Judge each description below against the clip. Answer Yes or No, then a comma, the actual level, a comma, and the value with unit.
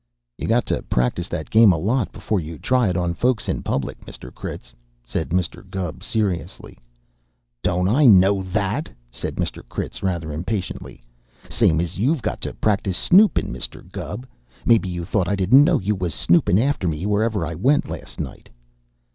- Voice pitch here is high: No, very low, 95 Hz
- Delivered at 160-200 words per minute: Yes, average, 175 wpm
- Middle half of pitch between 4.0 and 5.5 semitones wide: Yes, average, 4.4 semitones